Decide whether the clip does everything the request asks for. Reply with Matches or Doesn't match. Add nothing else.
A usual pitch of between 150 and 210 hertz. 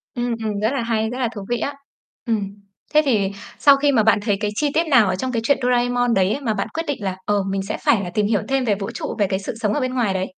Doesn't match